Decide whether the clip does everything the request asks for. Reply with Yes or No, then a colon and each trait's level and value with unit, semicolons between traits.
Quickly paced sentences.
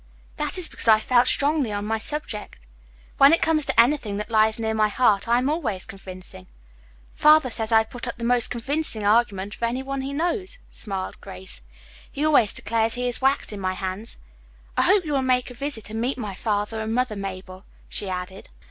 Yes: fast, 210 wpm